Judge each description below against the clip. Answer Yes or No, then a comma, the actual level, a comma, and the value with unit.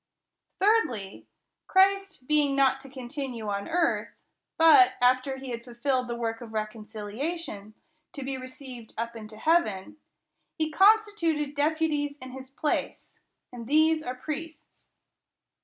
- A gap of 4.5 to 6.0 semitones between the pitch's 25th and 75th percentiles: Yes, average, 5.0 semitones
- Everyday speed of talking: No, slow, 125 wpm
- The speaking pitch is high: Yes, very high, 270 Hz